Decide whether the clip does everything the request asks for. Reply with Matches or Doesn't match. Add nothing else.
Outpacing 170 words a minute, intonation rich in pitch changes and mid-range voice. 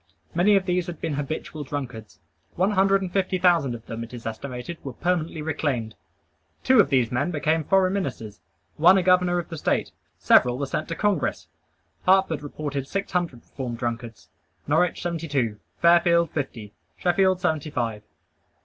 Doesn't match